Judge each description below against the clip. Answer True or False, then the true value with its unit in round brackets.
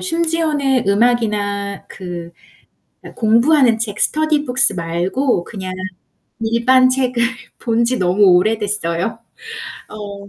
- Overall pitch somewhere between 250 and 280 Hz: False (225 Hz)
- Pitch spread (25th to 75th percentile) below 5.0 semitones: True (4.4 semitones)